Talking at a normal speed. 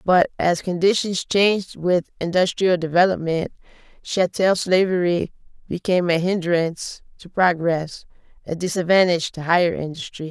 No: slow, 110 wpm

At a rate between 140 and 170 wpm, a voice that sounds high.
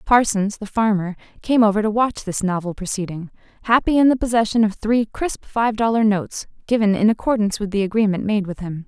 No: average, 195 wpm; high, 210 Hz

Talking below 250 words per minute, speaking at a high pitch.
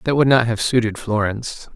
No: fast, 205 wpm; low, 115 Hz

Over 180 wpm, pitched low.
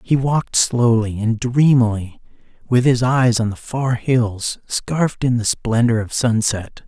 No: average, 155 wpm; low, 120 Hz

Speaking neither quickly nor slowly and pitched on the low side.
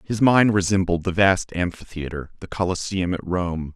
Yes: average, 160 wpm; very low, 90 Hz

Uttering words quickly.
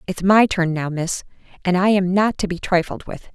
Yes: fast, 235 wpm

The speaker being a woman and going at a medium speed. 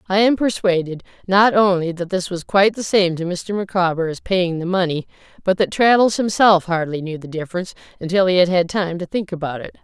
No: female; fast, 215 wpm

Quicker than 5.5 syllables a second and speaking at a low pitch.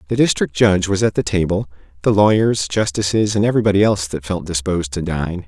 Yes: 6.3 syllables/s; very low, 95 Hz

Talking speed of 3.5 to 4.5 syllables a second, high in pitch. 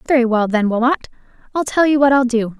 No: 6.0 syllables/s; very high, 250 Hz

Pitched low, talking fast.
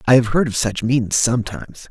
Yes: low, 120 Hz; fast, 220 wpm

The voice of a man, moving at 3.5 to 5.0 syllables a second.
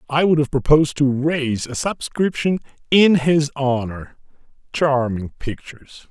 Yes: male; 4.4 syllables/s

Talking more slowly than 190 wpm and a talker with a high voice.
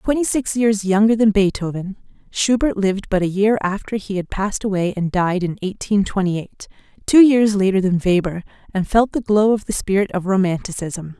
No: average, 195 wpm; high, 200 Hz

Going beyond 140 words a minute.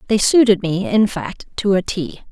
Yes: fast, 205 wpm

